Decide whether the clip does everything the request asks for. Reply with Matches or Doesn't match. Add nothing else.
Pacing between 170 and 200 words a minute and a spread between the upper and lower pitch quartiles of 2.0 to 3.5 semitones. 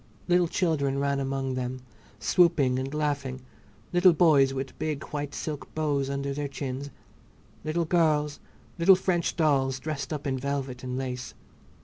Doesn't match